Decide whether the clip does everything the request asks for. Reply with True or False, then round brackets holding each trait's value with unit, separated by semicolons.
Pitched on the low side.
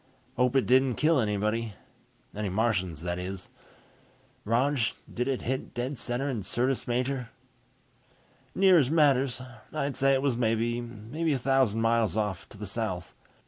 True (120 Hz)